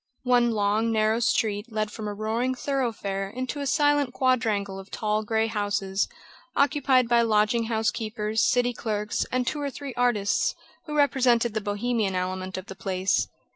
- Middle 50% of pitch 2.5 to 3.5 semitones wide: Yes, average, 3.1 semitones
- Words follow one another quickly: No, average, 165 wpm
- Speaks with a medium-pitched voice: No, high, 225 Hz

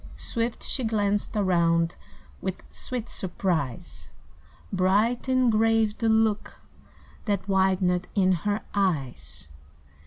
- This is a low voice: No, high, 195 Hz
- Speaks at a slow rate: Yes, slow, 100 wpm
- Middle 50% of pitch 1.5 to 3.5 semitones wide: No, average, 4.2 semitones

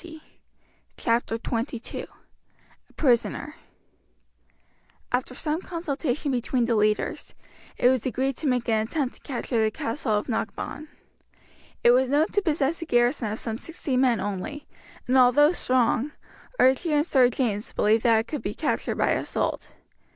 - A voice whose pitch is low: No, very high, 250 Hz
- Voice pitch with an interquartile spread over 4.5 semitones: No, average, 4.2 semitones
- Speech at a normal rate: Yes, average, 150 wpm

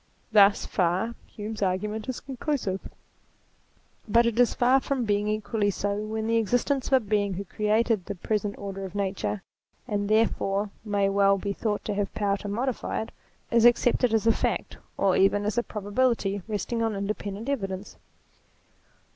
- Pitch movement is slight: Yes, narrow, 2.3 semitones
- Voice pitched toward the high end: Yes, high, 210 Hz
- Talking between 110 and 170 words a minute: Yes, average, 165 wpm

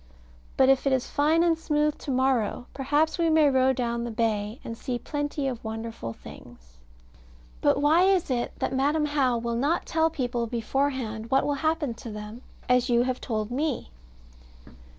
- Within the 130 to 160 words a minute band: No, average, 175 wpm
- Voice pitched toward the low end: No, very high, 260 Hz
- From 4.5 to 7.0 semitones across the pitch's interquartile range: No, average, 4.0 semitones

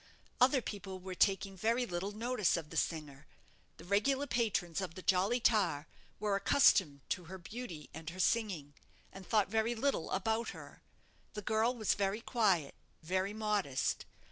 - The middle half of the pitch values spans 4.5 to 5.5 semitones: No, average, 4.1 semitones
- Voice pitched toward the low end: No, high, 195 Hz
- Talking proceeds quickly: No, average, 160 wpm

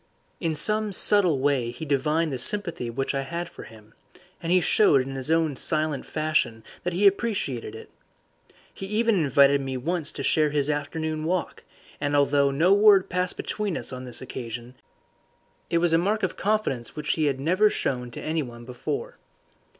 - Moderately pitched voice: Yes, medium, 155 Hz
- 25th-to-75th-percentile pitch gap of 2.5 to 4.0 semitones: No, average, 5.2 semitones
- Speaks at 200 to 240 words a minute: No, average, 180 wpm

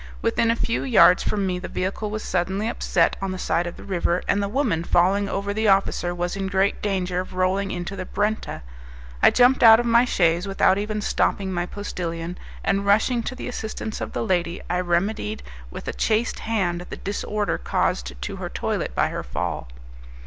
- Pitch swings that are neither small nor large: Yes, average, 3.2 semitones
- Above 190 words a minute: Yes, average, 200 wpm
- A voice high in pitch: Yes, high, 195 Hz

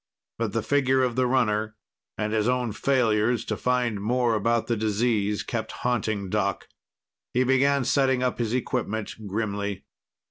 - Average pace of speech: Yes, average, 150 wpm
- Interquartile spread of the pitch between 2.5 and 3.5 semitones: Yes, average, 2.9 semitones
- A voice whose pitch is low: Yes, low, 115 Hz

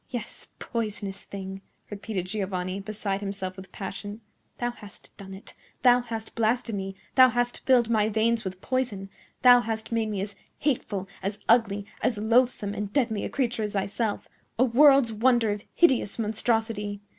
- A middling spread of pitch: Yes, average, 3.1 semitones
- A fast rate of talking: No, average, 155 wpm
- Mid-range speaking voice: No, high, 215 Hz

